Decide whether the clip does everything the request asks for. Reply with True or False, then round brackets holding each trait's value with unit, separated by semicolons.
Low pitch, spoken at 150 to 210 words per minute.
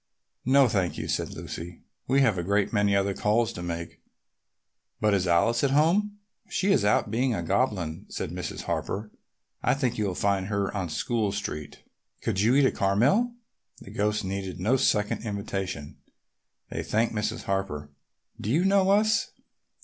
True (105 Hz; 170 wpm)